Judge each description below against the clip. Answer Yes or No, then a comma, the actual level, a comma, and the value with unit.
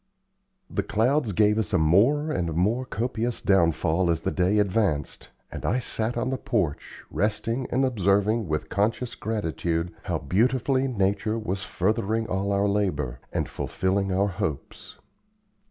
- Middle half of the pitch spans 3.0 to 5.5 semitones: Yes, average, 4.1 semitones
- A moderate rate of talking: Yes, average, 145 wpm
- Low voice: Yes, low, 100 Hz